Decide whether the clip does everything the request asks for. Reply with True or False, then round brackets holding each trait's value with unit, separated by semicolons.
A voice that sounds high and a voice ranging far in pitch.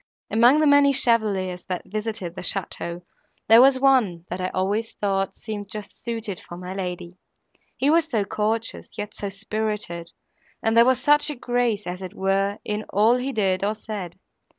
False (210 Hz; 3.8 semitones)